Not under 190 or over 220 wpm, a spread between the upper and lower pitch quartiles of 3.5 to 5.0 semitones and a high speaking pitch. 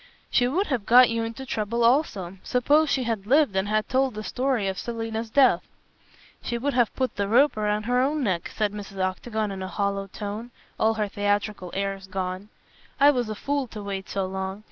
Yes: fast, 205 wpm; average, 3.9 semitones; high, 215 Hz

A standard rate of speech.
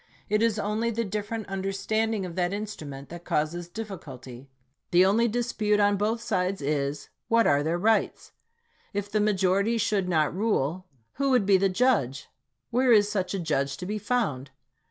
Yes: average, 175 wpm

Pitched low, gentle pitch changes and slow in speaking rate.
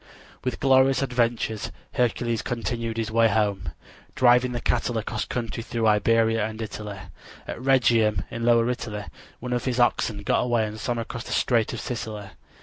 No: low, 115 Hz; narrow, 1.9 semitones; average, 165 wpm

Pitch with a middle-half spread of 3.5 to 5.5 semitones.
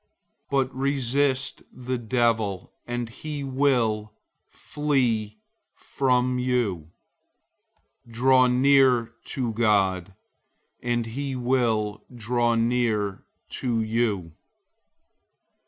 No: average, 2.9 semitones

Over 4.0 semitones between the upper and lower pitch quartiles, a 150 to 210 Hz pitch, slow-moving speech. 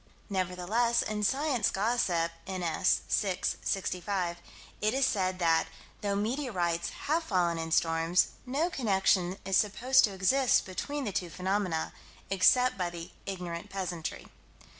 Yes: average, 4.8 semitones; high, 190 Hz; slow, 130 wpm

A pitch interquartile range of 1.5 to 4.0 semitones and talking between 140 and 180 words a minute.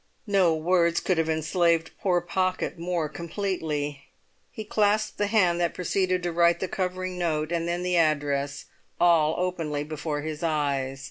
Yes: average, 2.9 semitones; average, 155 wpm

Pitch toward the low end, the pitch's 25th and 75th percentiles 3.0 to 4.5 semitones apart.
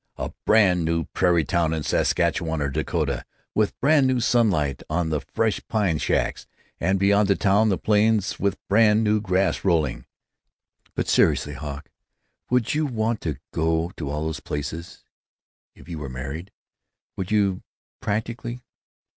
No: very low, 95 Hz; average, 5.2 semitones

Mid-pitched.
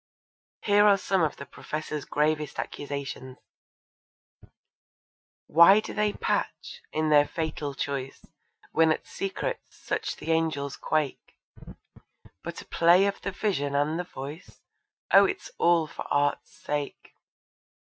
Yes: medium, 155 Hz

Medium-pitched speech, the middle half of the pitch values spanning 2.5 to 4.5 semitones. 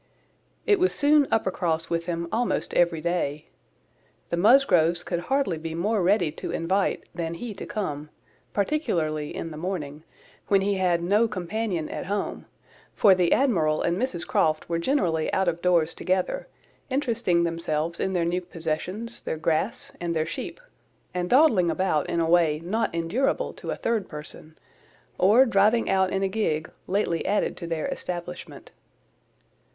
Yes: medium, 175 Hz; average, 3.9 semitones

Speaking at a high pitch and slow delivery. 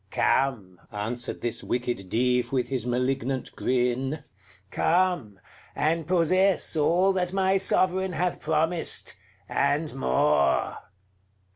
No: low, 135 Hz; slow, 105 wpm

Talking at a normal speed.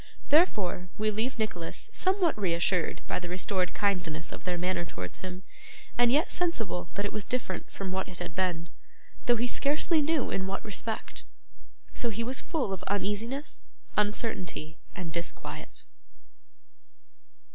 Yes: average, 145 wpm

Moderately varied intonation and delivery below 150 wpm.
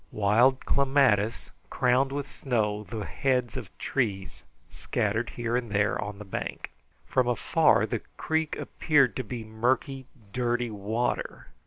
Yes: average, 3.7 semitones; slow, 135 wpm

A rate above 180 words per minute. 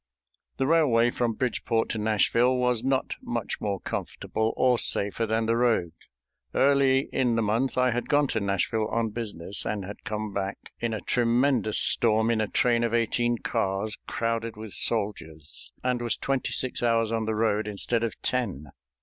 No: average, 175 wpm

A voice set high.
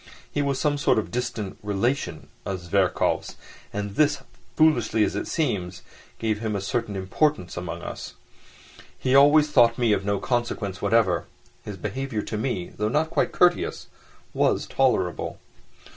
No: low, 110 Hz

